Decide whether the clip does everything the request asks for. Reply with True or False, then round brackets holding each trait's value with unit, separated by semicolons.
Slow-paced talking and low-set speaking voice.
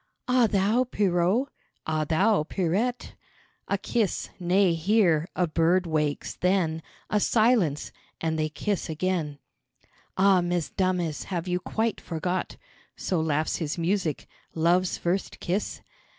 False (125 wpm; 180 Hz)